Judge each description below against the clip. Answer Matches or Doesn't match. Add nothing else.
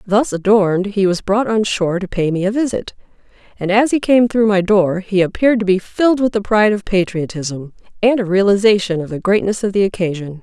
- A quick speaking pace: Matches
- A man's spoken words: Doesn't match